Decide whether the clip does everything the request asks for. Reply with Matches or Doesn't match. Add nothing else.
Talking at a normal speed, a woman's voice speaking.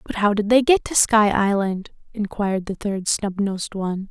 Matches